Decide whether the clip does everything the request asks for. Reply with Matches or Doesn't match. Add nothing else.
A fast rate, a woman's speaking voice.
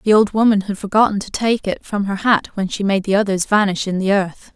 Matches